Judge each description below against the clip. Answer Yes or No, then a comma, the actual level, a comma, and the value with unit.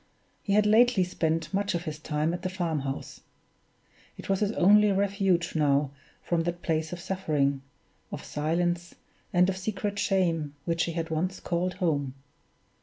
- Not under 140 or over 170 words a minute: Yes, average, 165 wpm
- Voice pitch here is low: No, medium, 175 Hz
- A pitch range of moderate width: Yes, average, 3.3 semitones